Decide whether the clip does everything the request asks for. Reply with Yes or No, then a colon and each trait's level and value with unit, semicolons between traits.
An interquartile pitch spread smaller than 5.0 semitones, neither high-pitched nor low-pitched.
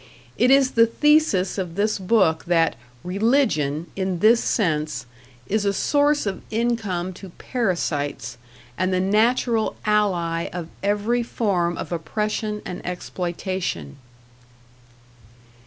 No: average, 4.6 semitones; high, 195 Hz